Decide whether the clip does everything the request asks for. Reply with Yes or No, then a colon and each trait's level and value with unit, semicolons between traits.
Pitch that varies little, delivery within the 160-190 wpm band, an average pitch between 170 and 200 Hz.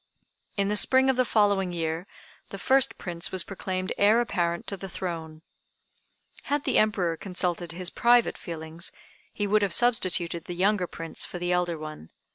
No: average, 3.5 semitones; average, 170 wpm; medium, 185 Hz